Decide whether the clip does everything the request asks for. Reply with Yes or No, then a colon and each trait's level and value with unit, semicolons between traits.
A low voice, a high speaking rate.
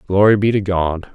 Yes: very low, 95 Hz; fast, 210 wpm